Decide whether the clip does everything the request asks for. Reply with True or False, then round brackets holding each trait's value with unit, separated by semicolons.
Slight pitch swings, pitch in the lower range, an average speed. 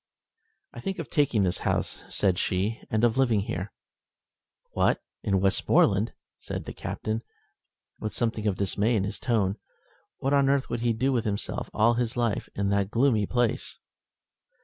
False (3.2 semitones; 110 Hz; 165 wpm)